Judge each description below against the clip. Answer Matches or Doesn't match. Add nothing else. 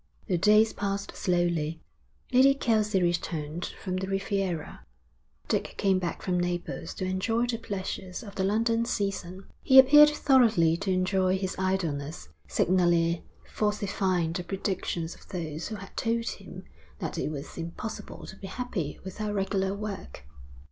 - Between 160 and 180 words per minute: Doesn't match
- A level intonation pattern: Doesn't match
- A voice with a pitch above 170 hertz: Matches